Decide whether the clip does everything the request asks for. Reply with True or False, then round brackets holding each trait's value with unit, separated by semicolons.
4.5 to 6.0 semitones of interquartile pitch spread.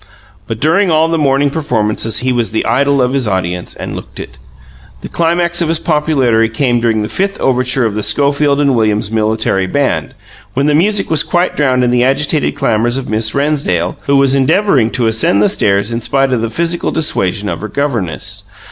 True (5.1 semitones)